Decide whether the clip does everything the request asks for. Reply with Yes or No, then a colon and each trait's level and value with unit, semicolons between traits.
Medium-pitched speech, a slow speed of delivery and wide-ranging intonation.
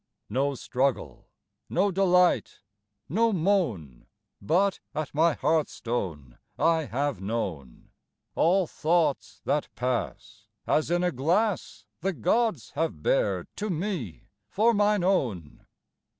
Yes: medium, 160 Hz; slow, 110 wpm; wide, 7.7 semitones